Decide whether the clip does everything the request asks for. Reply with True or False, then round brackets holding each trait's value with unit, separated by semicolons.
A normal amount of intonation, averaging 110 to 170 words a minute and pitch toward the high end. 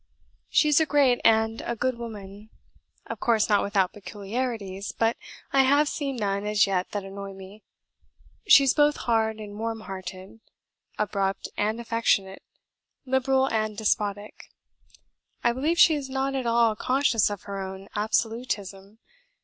True (4.0 semitones; 150 wpm; 220 Hz)